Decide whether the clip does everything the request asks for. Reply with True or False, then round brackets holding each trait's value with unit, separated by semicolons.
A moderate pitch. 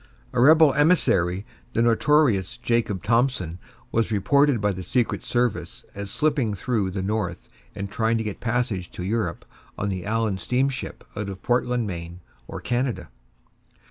False (115 Hz)